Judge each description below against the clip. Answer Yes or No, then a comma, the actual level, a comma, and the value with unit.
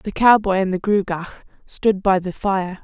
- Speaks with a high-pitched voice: Yes, high, 195 Hz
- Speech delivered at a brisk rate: No, average, 190 wpm